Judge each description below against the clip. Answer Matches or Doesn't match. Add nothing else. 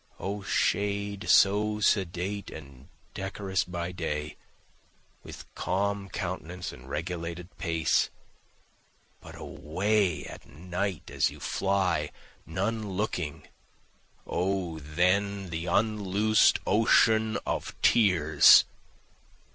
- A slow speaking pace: Matches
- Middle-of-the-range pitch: Doesn't match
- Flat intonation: Doesn't match